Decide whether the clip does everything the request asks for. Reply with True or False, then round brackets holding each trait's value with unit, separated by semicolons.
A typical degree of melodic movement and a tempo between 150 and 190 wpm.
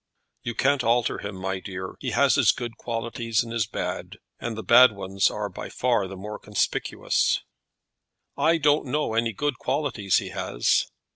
True (3.8 semitones; 170 wpm)